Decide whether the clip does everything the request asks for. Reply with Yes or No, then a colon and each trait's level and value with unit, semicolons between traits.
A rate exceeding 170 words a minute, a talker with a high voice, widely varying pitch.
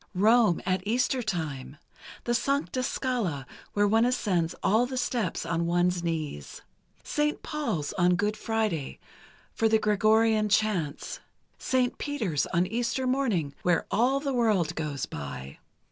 No: slow, 135 wpm; high, 210 Hz; wide, 6.1 semitones